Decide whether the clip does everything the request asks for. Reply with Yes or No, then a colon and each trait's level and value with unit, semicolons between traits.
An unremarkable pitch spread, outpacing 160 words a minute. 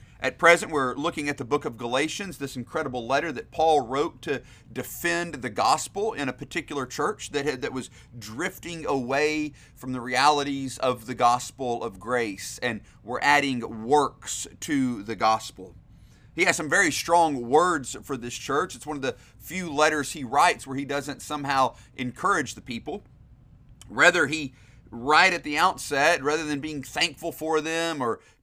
Yes: average, 3.7 semitones; average, 170 wpm